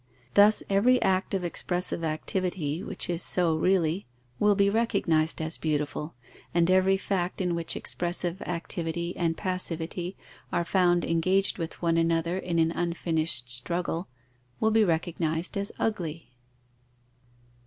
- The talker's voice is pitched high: No, medium, 175 Hz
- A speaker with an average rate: No, slow, 130 wpm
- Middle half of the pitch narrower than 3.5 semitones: Yes, narrow, 2.4 semitones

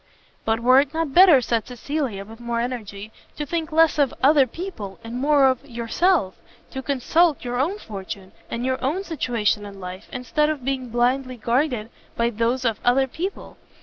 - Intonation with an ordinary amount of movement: Yes, average, 4.3 semitones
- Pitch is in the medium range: No, very high, 255 Hz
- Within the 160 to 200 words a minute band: Yes, average, 180 wpm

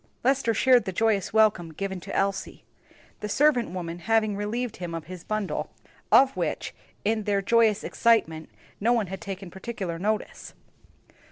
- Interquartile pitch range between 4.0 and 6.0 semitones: No, average, 3.5 semitones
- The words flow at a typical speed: Yes, average, 155 wpm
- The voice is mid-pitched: No, high, 205 Hz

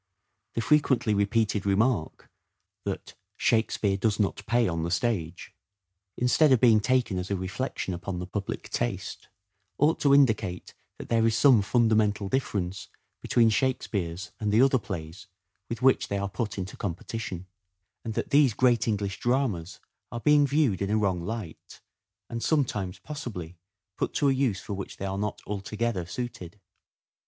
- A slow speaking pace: No, average, 160 wpm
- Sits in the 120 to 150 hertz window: No, low, 105 Hz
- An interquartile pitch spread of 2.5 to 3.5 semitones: No, average, 4.0 semitones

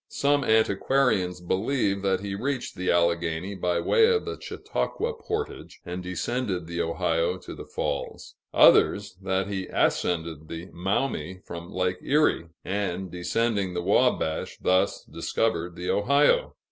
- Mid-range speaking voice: No, very low, 95 Hz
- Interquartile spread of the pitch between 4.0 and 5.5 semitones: Yes, average, 4.4 semitones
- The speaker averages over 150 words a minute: No, slow, 135 wpm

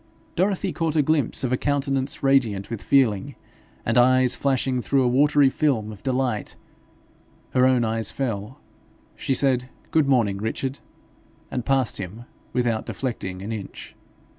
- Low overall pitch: Yes, low, 130 Hz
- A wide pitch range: No, average, 3.4 semitones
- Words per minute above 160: No, average, 145 wpm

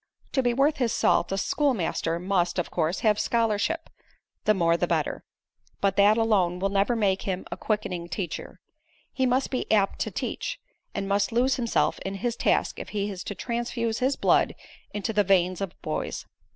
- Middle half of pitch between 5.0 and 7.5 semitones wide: No, average, 3.8 semitones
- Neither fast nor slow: Yes, average, 185 wpm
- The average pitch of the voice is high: Yes, high, 205 Hz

